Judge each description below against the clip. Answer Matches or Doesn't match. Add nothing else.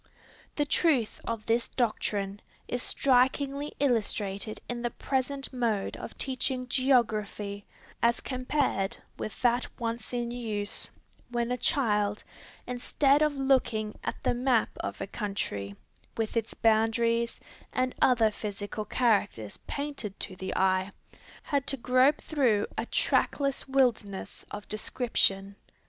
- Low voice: Doesn't match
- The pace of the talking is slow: Matches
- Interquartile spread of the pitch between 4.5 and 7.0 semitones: Doesn't match